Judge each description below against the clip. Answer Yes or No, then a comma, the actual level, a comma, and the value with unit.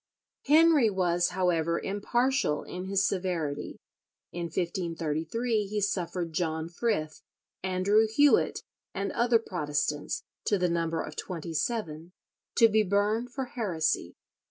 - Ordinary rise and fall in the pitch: Yes, average, 4.6 semitones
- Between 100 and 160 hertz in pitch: No, medium, 185 Hz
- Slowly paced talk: Yes, slow, 120 wpm